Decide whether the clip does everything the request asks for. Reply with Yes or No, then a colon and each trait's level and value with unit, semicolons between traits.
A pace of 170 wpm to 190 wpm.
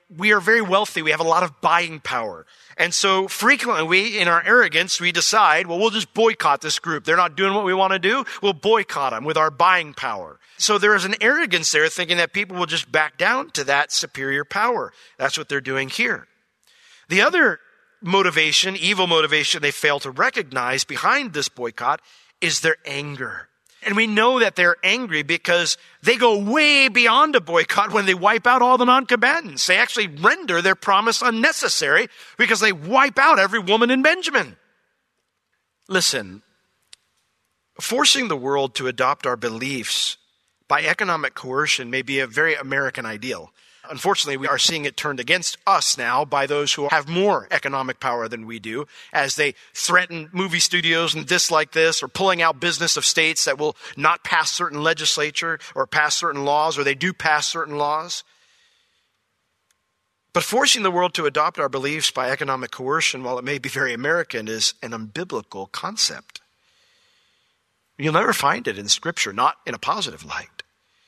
Yes: average, 180 wpm